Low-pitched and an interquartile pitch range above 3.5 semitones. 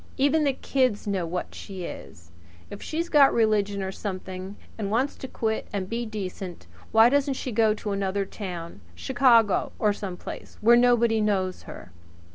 No: high, 210 Hz; average, 4.0 semitones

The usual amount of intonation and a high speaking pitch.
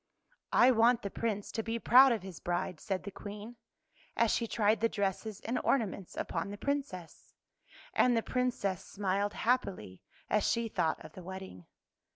Yes: average, 3.6 semitones; high, 210 Hz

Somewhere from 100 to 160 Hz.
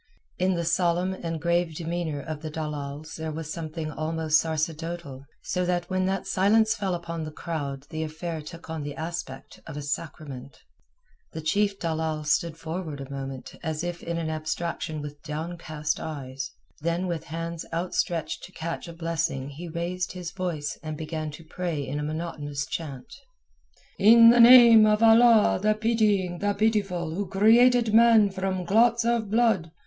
No: medium, 170 Hz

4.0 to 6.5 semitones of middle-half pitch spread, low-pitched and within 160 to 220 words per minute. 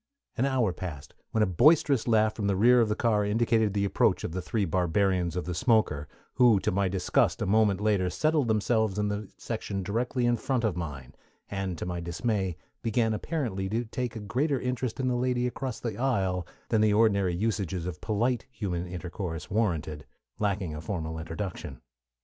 Yes: average, 4.3 semitones; low, 105 Hz; average, 190 wpm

